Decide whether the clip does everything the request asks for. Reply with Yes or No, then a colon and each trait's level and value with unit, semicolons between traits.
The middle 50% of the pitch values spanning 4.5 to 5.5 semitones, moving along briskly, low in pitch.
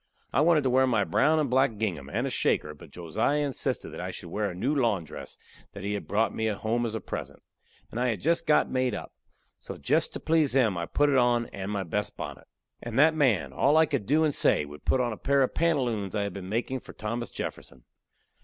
Yes: average, 5.2 semitones; fast, 245 wpm; low, 120 Hz